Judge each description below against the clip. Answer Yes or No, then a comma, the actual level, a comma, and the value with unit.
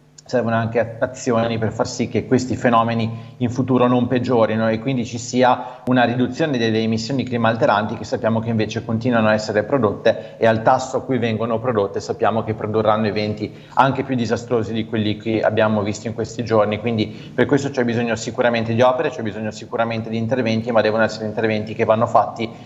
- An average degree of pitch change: No, narrow, 2.0 semitones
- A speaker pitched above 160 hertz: No, low, 115 Hz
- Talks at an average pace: No, fast, 195 wpm